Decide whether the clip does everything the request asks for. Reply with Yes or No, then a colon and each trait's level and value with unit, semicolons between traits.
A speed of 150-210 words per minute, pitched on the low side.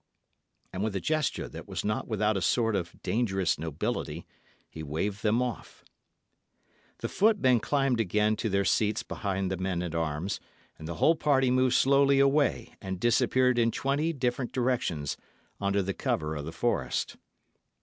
Yes: average, 160 wpm; low, 110 Hz